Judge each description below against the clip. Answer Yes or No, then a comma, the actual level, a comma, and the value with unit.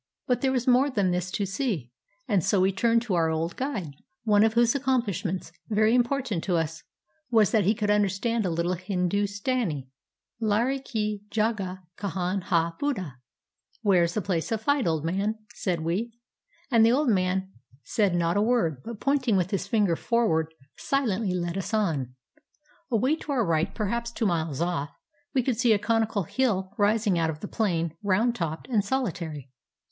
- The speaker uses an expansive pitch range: No, average, 5.0 semitones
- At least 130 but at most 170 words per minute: No, average, 185 wpm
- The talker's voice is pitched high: Yes, high, 205 Hz